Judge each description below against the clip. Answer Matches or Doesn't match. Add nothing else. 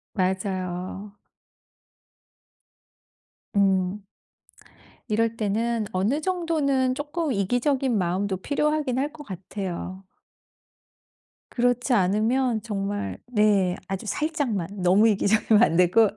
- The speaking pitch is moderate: Doesn't match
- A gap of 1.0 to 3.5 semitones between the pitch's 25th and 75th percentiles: Doesn't match